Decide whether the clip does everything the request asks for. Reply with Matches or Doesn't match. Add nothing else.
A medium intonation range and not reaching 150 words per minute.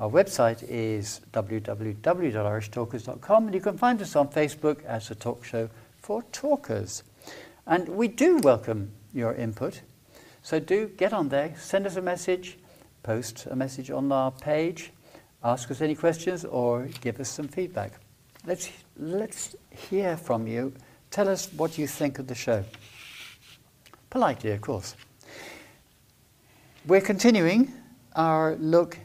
Doesn't match